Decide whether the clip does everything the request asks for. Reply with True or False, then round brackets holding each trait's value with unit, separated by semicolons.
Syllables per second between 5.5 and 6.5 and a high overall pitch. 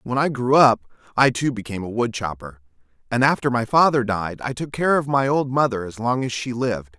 False (5.6 syllables/s; 120 Hz)